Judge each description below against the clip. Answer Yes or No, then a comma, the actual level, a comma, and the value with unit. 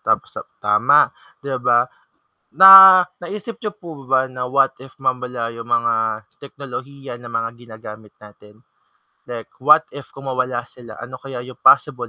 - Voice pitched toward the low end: Yes, low, 125 Hz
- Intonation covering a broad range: No, average, 2.9 semitones